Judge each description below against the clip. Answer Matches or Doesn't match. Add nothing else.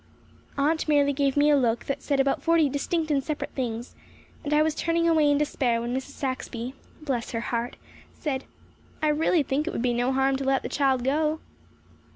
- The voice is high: Matches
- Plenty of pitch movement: Doesn't match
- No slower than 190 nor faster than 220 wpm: Matches